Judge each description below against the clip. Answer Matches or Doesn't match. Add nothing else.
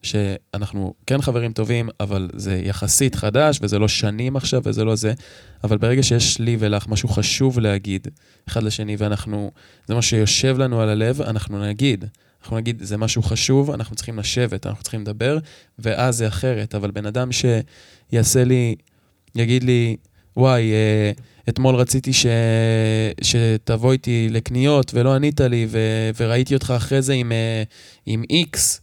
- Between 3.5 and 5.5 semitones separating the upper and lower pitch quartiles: Doesn't match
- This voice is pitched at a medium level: Doesn't match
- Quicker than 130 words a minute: Matches